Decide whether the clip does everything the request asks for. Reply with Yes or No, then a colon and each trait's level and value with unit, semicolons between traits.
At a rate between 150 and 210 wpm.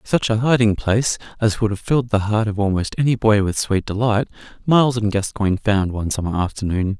Yes: fast, 205 wpm